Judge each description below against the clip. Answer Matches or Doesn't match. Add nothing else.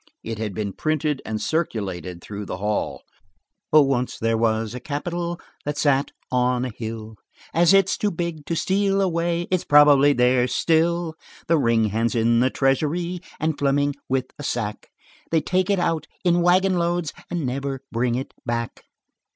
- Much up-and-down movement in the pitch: Matches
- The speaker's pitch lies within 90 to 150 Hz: Matches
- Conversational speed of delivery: Matches